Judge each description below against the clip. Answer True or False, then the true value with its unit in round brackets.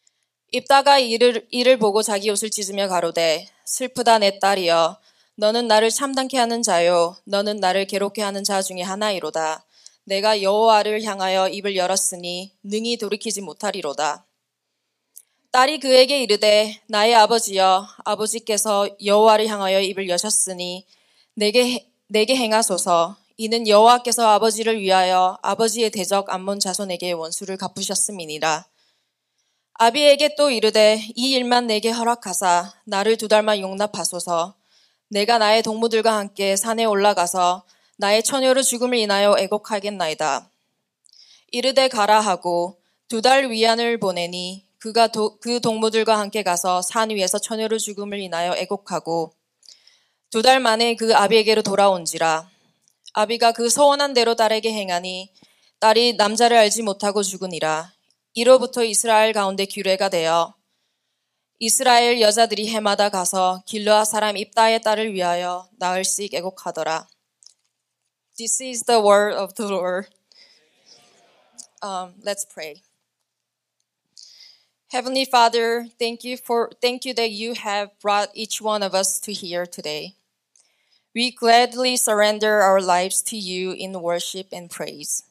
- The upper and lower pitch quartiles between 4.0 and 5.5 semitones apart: False (3.3 semitones)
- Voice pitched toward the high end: True (210 Hz)